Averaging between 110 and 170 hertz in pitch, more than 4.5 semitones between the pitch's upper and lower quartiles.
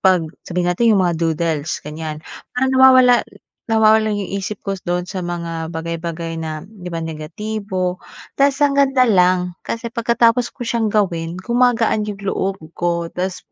No: medium, 185 Hz; average, 5.1 semitones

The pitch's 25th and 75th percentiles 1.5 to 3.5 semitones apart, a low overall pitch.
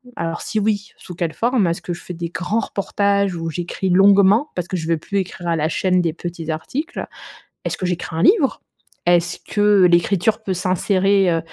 No: average, 2.9 semitones; medium, 185 Hz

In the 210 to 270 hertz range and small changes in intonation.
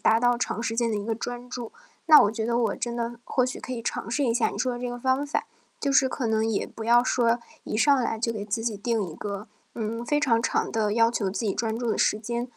Yes: high, 235 Hz; narrow, 1.7 semitones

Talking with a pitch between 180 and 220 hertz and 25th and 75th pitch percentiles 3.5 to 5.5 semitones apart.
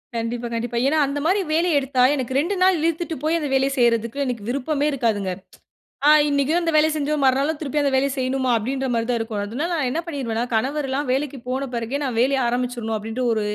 No: very high, 265 Hz; average, 3.8 semitones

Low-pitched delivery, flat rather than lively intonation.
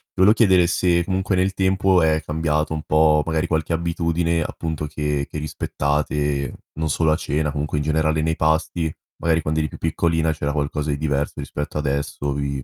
Yes: very low, 80 Hz; narrow, 2.0 semitones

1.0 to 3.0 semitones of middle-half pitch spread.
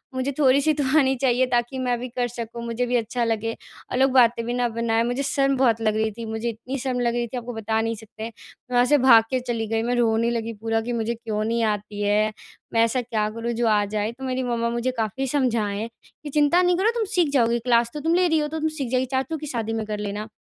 Yes: narrow, 2.6 semitones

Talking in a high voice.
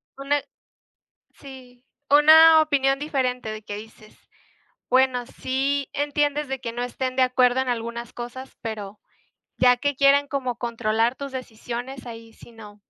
Yes: very high, 255 Hz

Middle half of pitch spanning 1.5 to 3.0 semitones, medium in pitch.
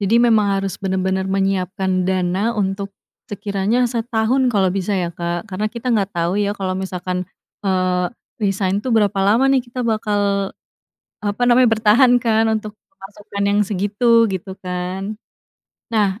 No: average, 2.7 semitones; high, 200 Hz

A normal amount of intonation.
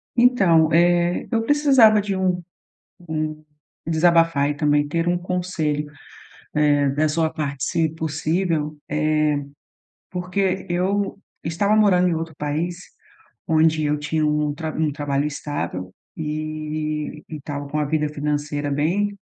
Yes: average, 3.1 semitones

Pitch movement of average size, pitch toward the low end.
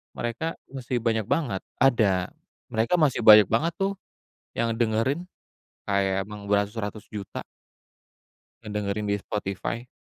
Yes: average, 3.1 semitones; low, 110 Hz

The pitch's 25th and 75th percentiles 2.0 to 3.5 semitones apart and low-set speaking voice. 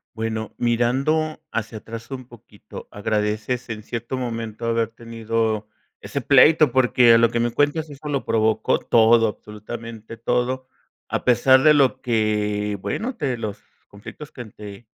Yes: average, 2.7 semitones; low, 115 Hz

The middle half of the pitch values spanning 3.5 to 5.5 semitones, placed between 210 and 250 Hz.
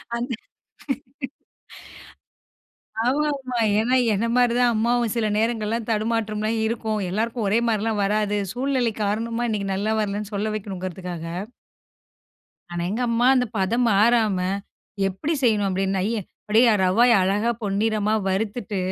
No: average, 2.7 semitones; high, 220 Hz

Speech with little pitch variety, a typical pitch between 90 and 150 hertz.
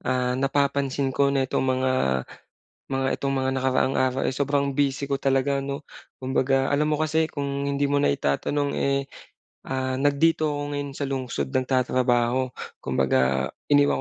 Yes: narrow, 1.6 semitones; low, 135 Hz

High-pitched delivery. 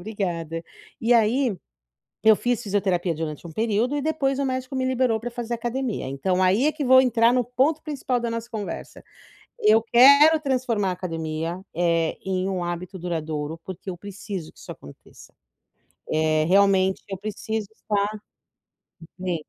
Yes: high, 205 Hz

